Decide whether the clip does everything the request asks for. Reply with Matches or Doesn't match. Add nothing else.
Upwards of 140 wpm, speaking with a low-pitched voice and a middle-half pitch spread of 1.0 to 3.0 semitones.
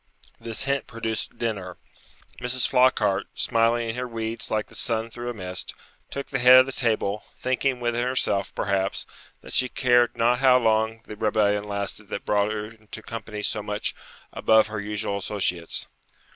Matches